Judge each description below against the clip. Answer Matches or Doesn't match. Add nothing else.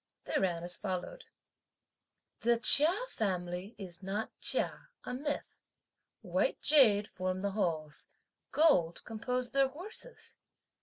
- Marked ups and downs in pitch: Matches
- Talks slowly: Matches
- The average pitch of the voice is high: Matches